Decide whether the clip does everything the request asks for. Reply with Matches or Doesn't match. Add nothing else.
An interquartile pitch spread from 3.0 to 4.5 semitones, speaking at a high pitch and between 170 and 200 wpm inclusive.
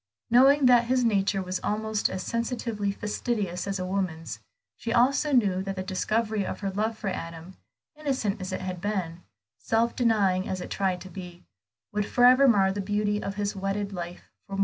Matches